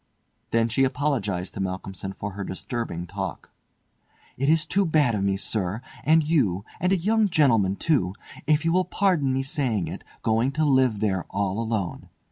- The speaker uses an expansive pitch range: Yes, wide, 7.7 semitones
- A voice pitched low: Yes, low, 115 Hz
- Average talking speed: Yes, average, 165 wpm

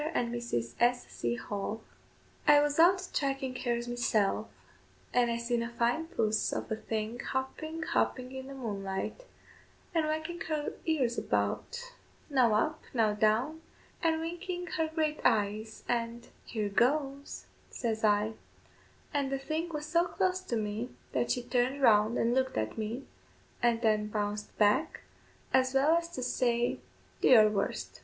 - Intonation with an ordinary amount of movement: No, wide, 5.7 semitones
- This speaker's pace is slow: No, average, 155 wpm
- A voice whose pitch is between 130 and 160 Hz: No, high, 245 Hz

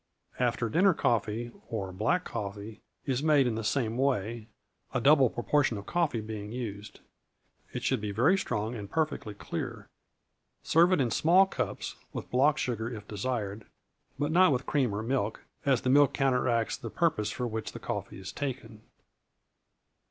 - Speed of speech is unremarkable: Yes, average, 165 wpm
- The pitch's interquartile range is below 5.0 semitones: Yes, average, 4.6 semitones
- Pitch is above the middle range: No, low, 120 Hz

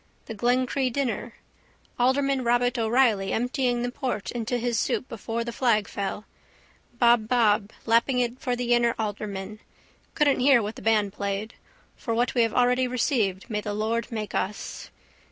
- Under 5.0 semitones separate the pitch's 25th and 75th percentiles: Yes, narrow, 2.6 semitones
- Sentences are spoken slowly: No, average, 155 wpm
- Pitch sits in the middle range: No, high, 235 Hz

